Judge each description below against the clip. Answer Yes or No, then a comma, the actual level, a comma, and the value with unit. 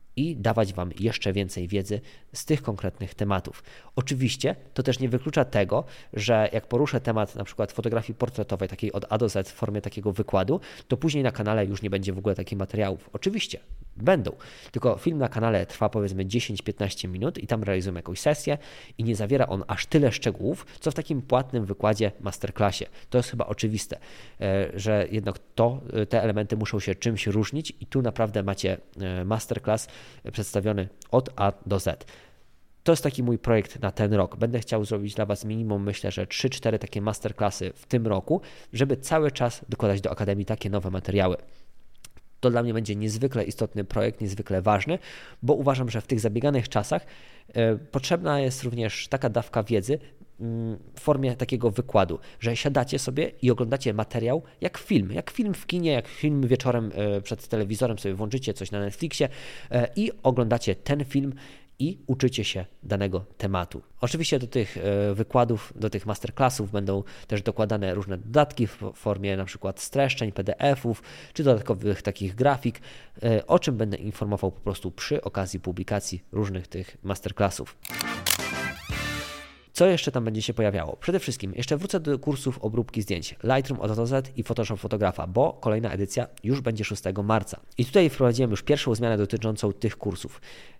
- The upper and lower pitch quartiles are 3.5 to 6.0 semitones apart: Yes, average, 4.0 semitones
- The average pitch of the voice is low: Yes, low, 110 Hz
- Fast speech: Yes, fast, 165 wpm